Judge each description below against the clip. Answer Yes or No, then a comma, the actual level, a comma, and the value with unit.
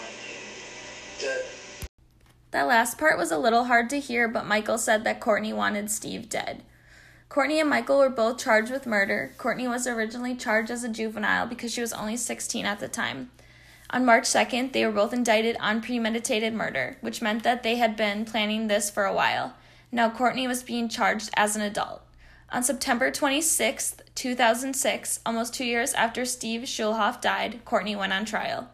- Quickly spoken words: No, average, 180 wpm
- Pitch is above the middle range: Yes, high, 230 Hz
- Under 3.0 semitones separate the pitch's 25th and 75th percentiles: Yes, narrow, 2.4 semitones